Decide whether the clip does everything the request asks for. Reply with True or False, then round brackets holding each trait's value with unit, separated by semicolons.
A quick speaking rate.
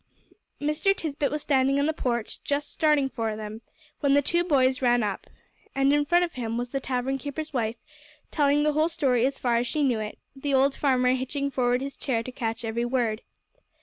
True (210 wpm)